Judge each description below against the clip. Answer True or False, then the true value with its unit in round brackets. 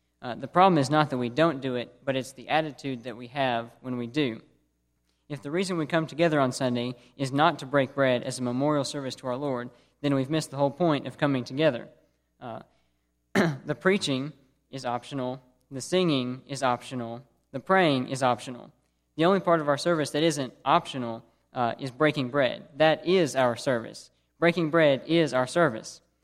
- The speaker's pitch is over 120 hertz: True (135 Hz)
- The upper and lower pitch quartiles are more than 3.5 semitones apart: True (3.9 semitones)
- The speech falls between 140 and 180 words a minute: False (190 wpm)